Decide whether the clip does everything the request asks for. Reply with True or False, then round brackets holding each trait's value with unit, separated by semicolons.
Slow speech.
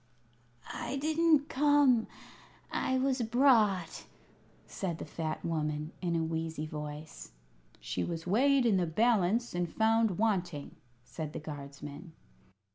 True (120 wpm)